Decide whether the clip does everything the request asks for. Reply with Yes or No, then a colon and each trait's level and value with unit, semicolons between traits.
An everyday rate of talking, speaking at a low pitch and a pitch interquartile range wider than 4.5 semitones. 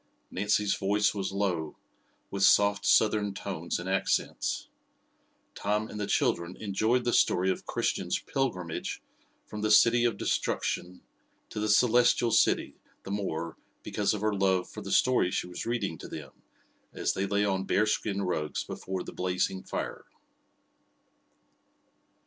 No: average, 145 wpm; low, 100 Hz; narrow, 2.4 semitones